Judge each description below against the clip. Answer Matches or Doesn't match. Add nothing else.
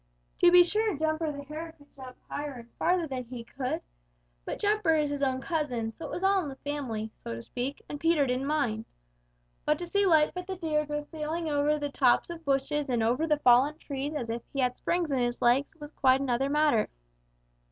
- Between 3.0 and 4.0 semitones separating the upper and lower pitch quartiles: Matches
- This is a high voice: Matches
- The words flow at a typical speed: Doesn't match